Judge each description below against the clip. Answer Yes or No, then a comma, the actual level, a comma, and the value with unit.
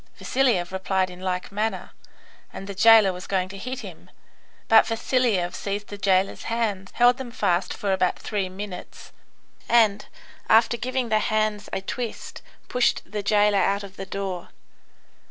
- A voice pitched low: No, high, 205 Hz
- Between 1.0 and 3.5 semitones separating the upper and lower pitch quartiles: Yes, average, 2.9 semitones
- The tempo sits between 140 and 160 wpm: Yes, average, 155 wpm